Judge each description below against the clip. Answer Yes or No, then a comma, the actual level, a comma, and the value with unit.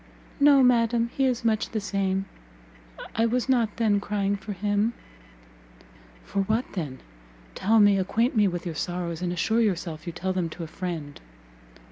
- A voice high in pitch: Yes, high, 205 Hz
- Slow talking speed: No, average, 165 wpm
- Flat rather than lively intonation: No, average, 4.2 semitones